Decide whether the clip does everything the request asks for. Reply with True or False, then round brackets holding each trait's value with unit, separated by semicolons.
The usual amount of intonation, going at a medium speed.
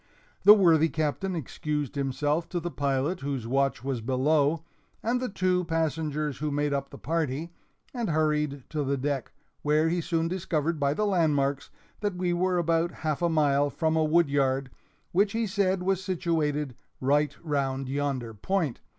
True (3.6 semitones; 165 wpm)